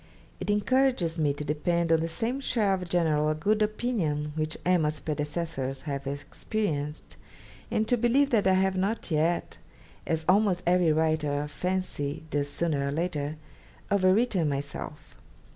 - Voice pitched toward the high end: No, medium, 165 Hz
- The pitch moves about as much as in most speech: Yes, average, 4.6 semitones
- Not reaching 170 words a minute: Yes, average, 145 wpm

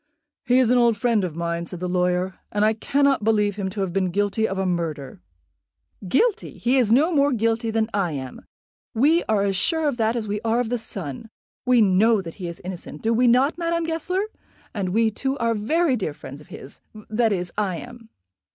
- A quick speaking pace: Yes, fast, 215 wpm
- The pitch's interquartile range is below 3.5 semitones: No, average, 4.9 semitones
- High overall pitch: Yes, high, 220 Hz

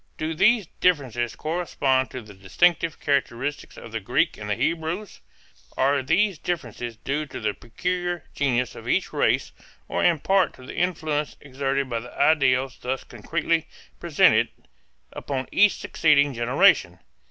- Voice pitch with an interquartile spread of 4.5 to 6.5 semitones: Yes, average, 4.8 semitones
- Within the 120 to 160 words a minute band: Yes, average, 145 wpm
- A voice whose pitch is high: No, medium, 140 Hz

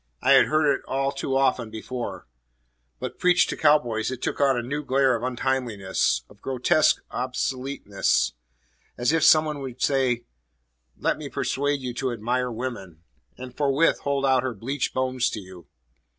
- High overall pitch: No, low, 130 Hz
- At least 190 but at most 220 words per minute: No, average, 165 wpm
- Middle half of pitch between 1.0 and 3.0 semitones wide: Yes, average, 2.7 semitones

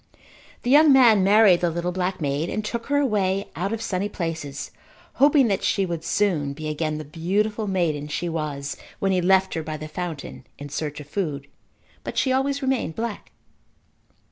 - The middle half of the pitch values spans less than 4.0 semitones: No, wide, 5.6 semitones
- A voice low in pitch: No, medium, 180 Hz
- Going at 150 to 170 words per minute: No, average, 185 wpm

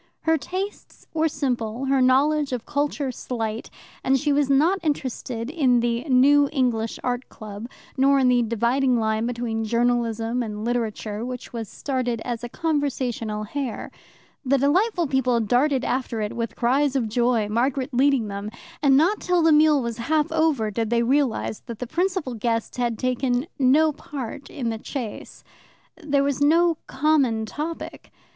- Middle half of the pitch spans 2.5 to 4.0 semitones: Yes, average, 3.7 semitones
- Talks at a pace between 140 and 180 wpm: Yes, average, 160 wpm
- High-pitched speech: Yes, very high, 255 Hz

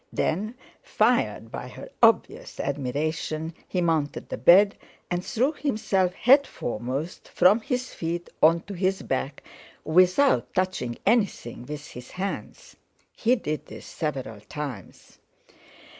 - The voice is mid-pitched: Yes, medium, 175 Hz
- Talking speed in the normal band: No, slow, 125 wpm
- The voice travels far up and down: Yes, wide, 6.5 semitones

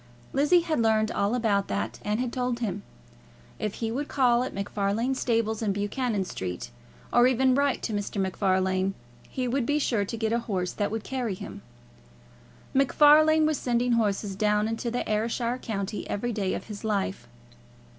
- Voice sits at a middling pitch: No, high, 225 Hz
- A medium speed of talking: Yes, average, 175 wpm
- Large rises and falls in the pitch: No, average, 3.7 semitones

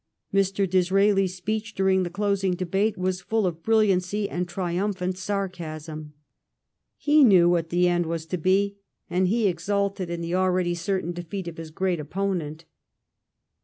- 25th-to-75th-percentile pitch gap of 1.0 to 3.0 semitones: Yes, narrow, 2.4 semitones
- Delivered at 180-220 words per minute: No, average, 150 wpm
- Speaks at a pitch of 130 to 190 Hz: Yes, medium, 185 Hz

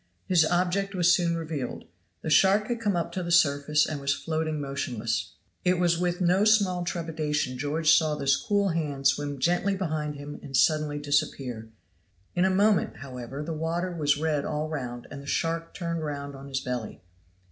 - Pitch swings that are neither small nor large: Yes, average, 3.7 semitones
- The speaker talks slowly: No, average, 180 wpm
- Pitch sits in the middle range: Yes, medium, 155 Hz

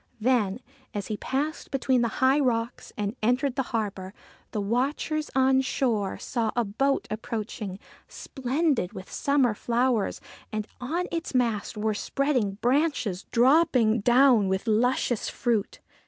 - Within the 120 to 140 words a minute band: Yes, slow, 135 wpm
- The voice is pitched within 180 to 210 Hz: No, high, 240 Hz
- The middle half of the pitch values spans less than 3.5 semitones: No, average, 3.8 semitones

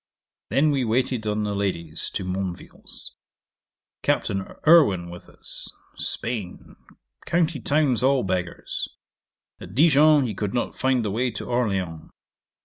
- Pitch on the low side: Yes, low, 110 Hz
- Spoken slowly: Yes, slow, 130 wpm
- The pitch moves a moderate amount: No, wide, 6.0 semitones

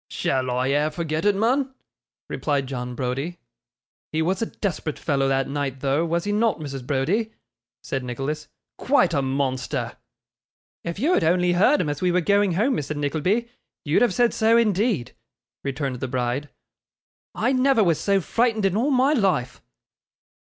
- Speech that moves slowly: No, average, 165 wpm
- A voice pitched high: No, medium, 165 Hz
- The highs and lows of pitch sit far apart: Yes, wide, 7.6 semitones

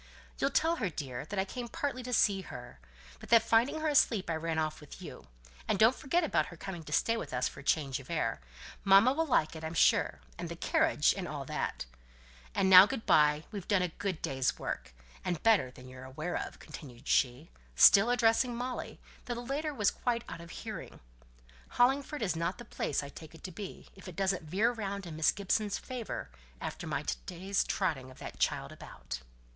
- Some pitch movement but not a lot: No, wide, 7.2 semitones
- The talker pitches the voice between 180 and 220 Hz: Yes, high, 190 Hz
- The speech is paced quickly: Yes, fast, 210 wpm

